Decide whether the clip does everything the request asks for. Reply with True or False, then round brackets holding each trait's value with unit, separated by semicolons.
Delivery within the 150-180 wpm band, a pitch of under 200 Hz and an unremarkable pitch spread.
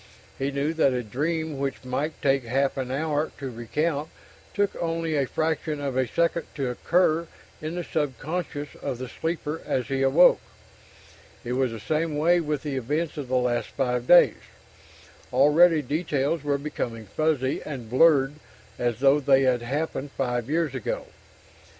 True (165 wpm; 140 Hz; 3.5 semitones)